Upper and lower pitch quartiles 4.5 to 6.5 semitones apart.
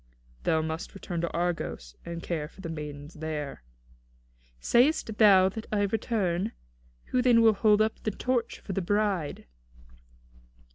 Yes: average, 5.0 semitones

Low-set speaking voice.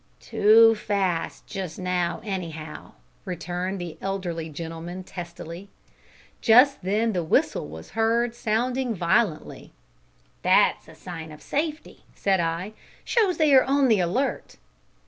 No: high, 190 Hz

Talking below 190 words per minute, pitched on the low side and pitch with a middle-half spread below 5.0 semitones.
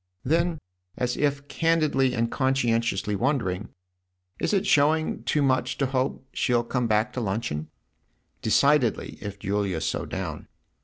No: average, 150 wpm; low, 125 Hz; wide, 5.4 semitones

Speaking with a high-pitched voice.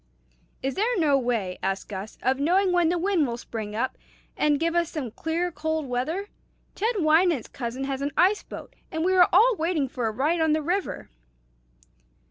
Yes: very high, 315 Hz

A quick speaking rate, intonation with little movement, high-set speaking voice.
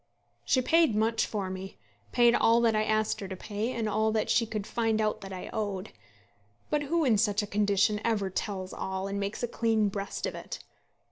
Yes: fast, 210 wpm; narrow, 2.3 semitones; high, 215 Hz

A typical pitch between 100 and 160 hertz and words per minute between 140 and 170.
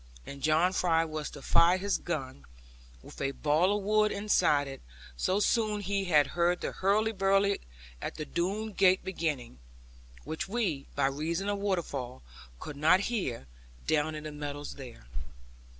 No: medium, 170 Hz; average, 160 wpm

